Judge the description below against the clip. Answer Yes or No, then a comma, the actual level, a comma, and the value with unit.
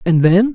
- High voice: Yes, high, 195 Hz